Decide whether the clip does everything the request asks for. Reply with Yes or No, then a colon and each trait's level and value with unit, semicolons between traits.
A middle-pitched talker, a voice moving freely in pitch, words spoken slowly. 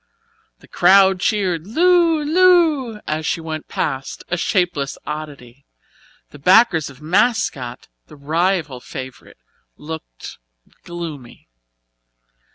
Yes: medium, 170 Hz; wide, 6.6 semitones; slow, 100 wpm